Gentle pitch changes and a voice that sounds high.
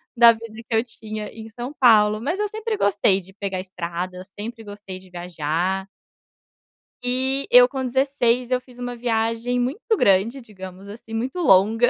No: average, 4.2 semitones; high, 225 Hz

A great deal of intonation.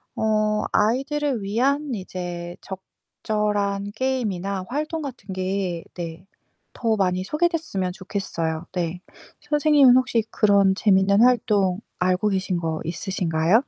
No: average, 4.9 semitones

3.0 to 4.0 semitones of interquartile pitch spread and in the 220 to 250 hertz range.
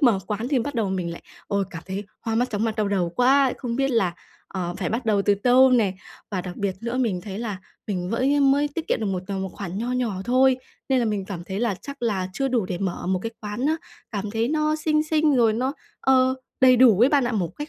No: average, 4.9 semitones; high, 225 Hz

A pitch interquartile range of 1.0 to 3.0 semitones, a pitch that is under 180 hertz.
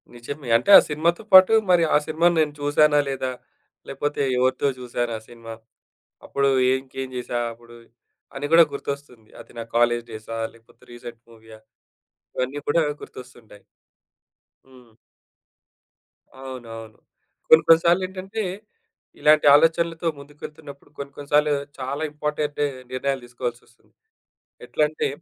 No: average, 4.1 semitones; medium, 140 Hz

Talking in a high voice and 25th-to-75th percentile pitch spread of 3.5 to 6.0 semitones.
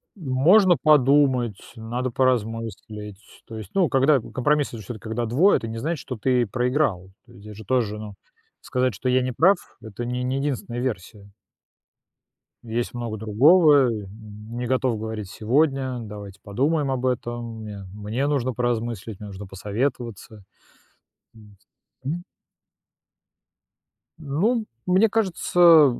No: low, 120 Hz; average, 4.1 semitones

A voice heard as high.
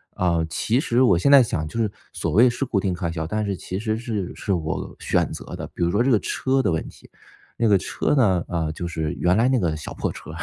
No: low, 100 Hz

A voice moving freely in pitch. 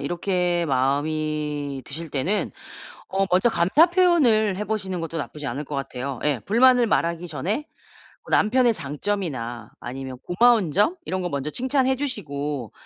Yes: wide, 7.2 semitones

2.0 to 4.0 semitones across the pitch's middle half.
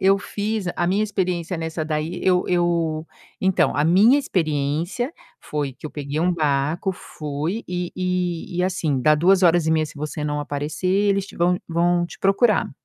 Yes: average, 3.3 semitones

